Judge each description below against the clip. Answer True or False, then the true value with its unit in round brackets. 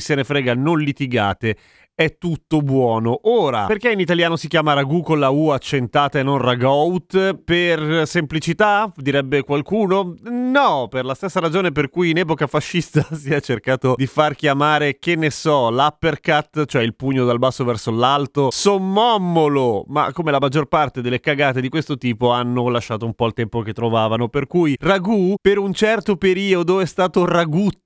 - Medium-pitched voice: True (150 Hz)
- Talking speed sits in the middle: False (175 wpm)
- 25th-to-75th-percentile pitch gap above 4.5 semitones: True (4.9 semitones)